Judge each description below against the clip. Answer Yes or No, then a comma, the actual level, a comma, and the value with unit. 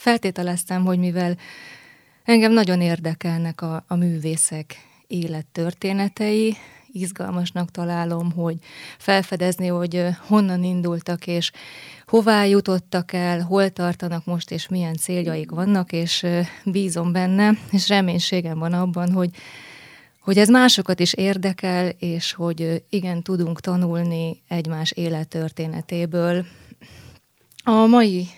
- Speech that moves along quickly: No, slow, 105 wpm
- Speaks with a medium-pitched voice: Yes, medium, 175 Hz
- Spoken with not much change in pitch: Yes, narrow, 2.1 semitones